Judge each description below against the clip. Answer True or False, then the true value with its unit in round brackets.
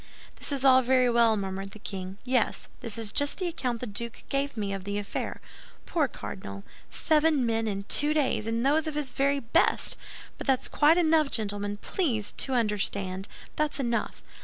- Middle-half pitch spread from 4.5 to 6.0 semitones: True (5.6 semitones)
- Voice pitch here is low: False (240 Hz)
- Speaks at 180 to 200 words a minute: True (185 wpm)